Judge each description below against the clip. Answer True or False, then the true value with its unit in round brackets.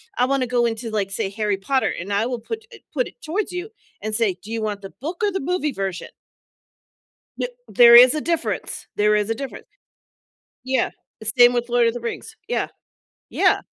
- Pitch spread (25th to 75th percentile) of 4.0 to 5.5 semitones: True (4.7 semitones)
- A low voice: False (240 Hz)